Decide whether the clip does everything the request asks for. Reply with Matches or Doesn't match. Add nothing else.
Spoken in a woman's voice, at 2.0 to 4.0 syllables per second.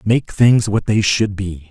Doesn't match